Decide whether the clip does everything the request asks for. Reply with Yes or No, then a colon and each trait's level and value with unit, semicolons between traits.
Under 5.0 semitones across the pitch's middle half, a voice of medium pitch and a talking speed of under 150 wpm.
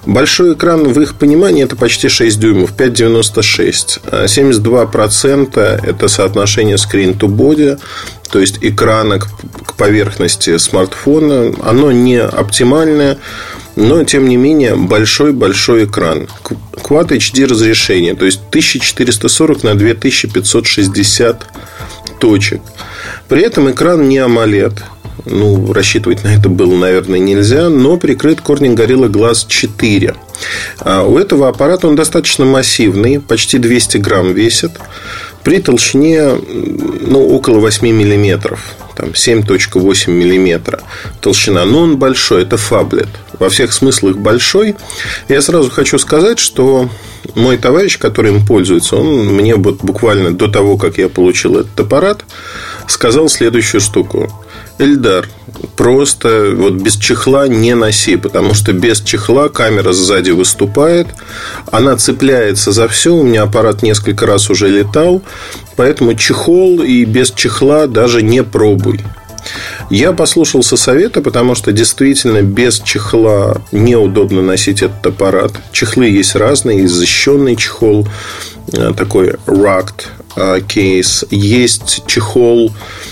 No: average, 4.6 semitones; low, 110 Hz; average, 120 wpm